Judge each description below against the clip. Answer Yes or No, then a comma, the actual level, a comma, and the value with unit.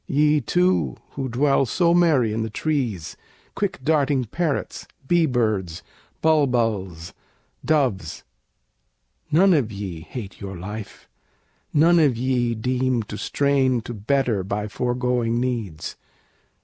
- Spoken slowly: Yes, slow, 120 wpm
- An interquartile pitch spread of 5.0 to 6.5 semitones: Yes, average, 5.3 semitones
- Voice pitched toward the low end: Yes, low, 125 Hz